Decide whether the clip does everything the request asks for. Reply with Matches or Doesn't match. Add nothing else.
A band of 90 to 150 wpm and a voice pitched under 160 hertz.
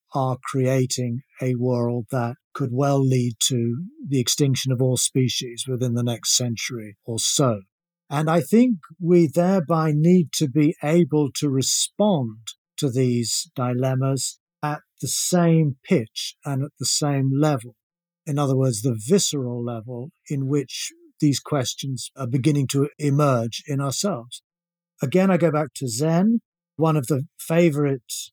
Matches